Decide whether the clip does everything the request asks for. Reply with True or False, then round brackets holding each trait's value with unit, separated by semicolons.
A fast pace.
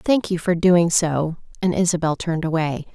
False (185 wpm)